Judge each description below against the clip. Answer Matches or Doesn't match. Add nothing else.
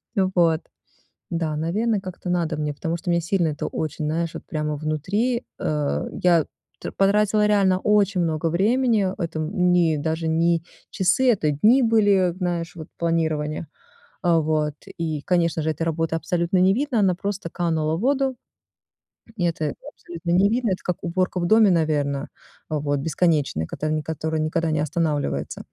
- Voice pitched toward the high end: Doesn't match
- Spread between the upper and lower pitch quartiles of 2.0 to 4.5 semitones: Matches